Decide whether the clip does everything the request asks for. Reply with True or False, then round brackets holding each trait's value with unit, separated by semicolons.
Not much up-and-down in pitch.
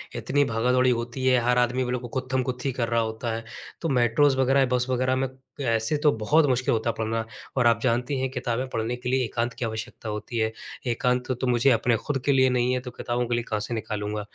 True (2.0 semitones)